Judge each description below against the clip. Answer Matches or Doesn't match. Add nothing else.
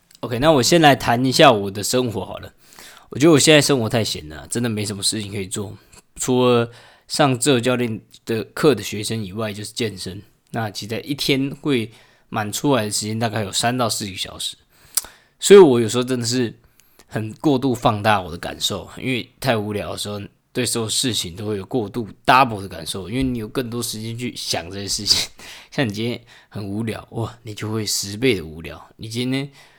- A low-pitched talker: Matches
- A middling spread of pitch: Matches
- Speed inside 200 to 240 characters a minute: Doesn't match